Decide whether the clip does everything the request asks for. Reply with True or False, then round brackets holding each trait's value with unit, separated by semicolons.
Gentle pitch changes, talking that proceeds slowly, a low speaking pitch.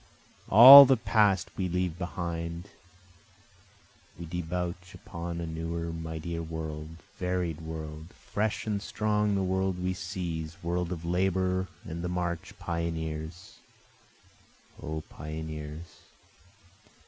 True (2.2 semitones; 110 wpm; 85 Hz)